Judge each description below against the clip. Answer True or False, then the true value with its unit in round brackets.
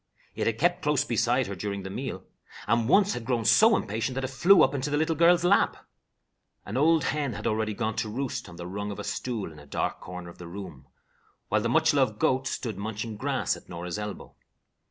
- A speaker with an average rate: False (225 wpm)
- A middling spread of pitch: False (5.8 semitones)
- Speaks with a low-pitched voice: True (115 Hz)